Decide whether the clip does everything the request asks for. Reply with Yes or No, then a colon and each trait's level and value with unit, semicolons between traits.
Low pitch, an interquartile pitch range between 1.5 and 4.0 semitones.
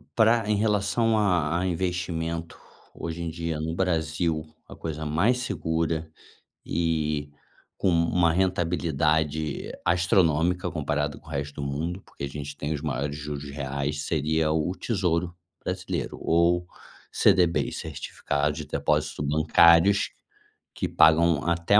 Yes: very low, 80 Hz; average, 2.8 semitones